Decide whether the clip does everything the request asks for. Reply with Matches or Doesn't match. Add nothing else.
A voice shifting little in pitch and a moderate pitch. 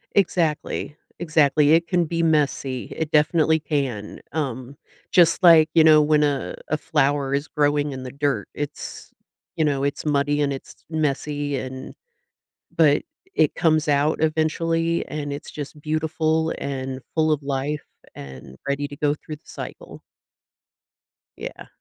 Matches